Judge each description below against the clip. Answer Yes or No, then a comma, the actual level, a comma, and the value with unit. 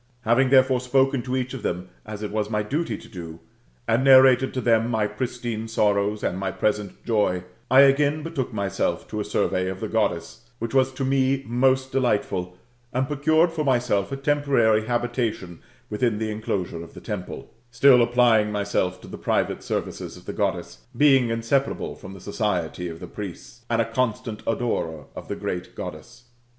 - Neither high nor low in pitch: No, low, 115 Hz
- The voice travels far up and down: No, average, 4.1 semitones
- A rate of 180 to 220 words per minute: Yes, average, 185 wpm